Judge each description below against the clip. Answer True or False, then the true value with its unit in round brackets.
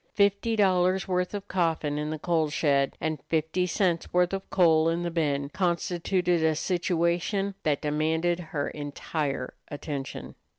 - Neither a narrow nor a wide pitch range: True (3.0 semitones)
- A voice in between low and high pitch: True (170 Hz)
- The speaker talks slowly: False (145 wpm)